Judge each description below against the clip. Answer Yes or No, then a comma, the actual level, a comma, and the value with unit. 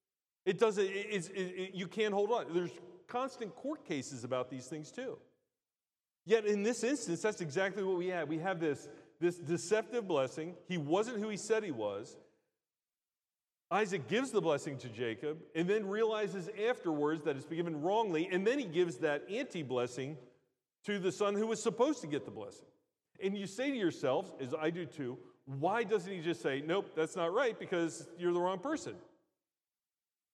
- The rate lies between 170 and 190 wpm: Yes, average, 185 wpm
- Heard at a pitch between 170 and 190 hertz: Yes, medium, 185 Hz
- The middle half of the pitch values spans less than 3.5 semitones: No, average, 5.1 semitones